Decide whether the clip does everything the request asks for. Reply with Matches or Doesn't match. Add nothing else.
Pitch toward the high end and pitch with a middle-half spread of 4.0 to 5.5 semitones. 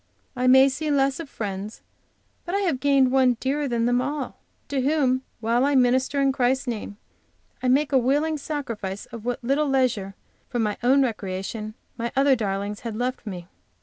Doesn't match